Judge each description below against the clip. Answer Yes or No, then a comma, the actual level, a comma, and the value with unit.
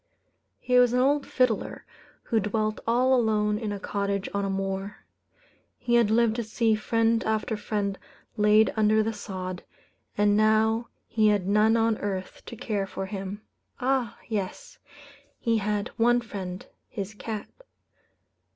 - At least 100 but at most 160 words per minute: Yes, average, 150 wpm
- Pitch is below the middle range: No, high, 215 Hz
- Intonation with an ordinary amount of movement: No, narrow, 2.1 semitones